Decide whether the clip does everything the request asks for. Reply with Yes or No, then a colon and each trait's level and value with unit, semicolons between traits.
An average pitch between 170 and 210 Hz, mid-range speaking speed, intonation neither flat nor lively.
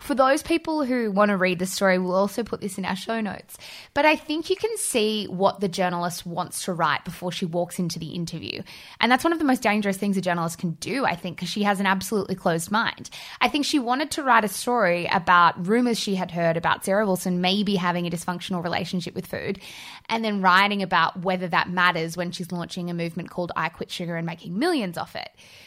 No: high, 190 Hz; fast, 235 wpm; average, 4.0 semitones